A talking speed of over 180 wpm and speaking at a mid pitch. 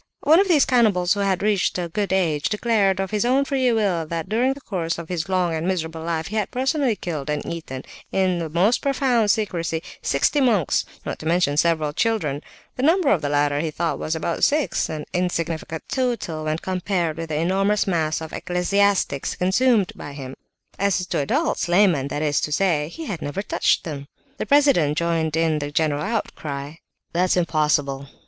Yes: average, 190 wpm; medium, 175 Hz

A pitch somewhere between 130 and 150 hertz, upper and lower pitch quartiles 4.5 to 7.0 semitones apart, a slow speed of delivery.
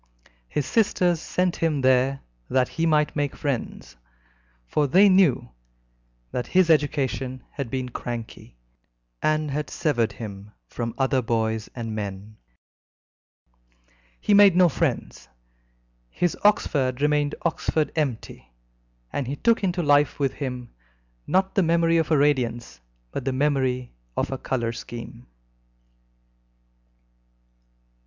Yes: medium, 140 Hz; average, 4.9 semitones; slow, 120 wpm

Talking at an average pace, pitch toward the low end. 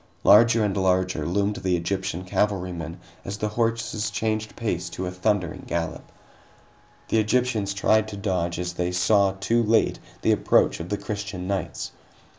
Yes: average, 155 wpm; low, 100 Hz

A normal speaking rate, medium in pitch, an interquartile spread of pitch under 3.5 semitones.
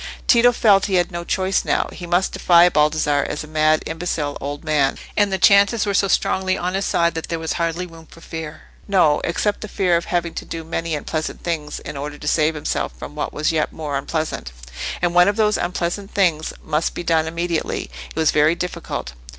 No: fast, 215 wpm; medium, 170 Hz; average, 3.0 semitones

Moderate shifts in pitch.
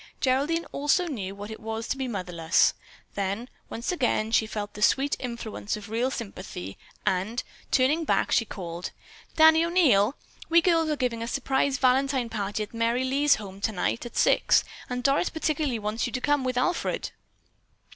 Yes: average, 4.9 semitones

